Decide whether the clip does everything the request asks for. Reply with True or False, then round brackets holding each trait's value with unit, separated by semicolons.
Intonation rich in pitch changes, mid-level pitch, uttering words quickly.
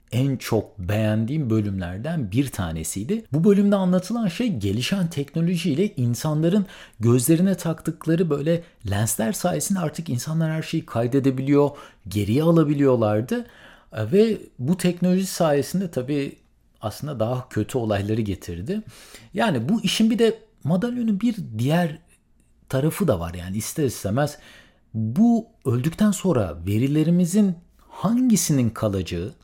False (8.6 semitones; 150 Hz; 110 wpm)